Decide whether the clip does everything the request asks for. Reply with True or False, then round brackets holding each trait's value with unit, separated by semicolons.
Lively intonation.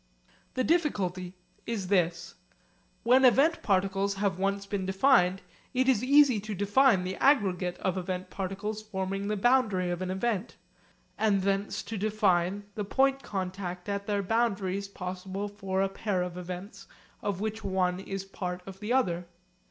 False (2.5 semitones)